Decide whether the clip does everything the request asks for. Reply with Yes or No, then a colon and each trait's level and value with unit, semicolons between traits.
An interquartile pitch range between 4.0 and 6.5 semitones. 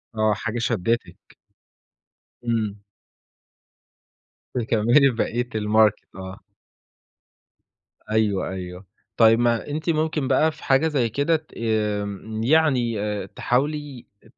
Yes: average, 4.3 semitones